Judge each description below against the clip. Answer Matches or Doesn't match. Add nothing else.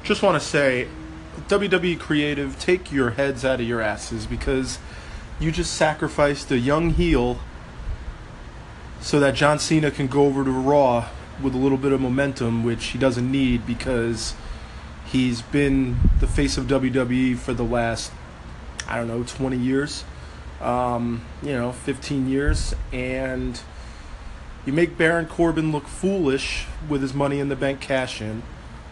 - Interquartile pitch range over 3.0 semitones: Matches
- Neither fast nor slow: Matches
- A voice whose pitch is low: Matches